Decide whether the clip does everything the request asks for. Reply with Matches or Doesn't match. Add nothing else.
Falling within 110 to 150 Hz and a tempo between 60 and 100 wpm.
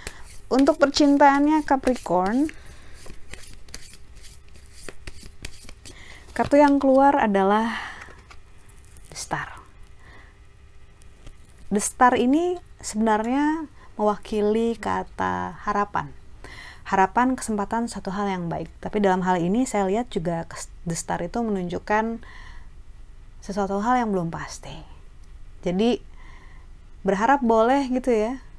Doesn't match